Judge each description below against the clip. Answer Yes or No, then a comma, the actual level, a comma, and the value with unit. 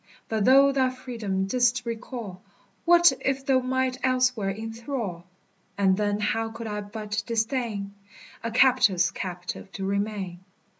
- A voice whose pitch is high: Yes, high, 225 Hz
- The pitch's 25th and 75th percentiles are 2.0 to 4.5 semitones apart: Yes, average, 4.2 semitones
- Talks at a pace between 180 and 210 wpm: No, slow, 135 wpm